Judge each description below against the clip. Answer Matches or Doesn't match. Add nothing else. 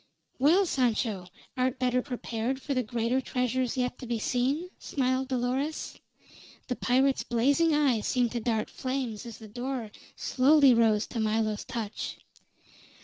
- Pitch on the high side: Matches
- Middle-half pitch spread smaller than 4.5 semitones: Matches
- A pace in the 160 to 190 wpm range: Doesn't match